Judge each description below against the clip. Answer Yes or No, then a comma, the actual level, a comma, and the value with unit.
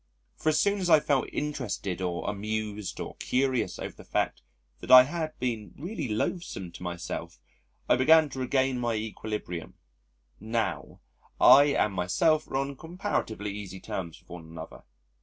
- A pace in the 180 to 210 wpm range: No, average, 160 wpm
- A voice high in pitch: No, low, 120 Hz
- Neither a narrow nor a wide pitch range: No, wide, 6.6 semitones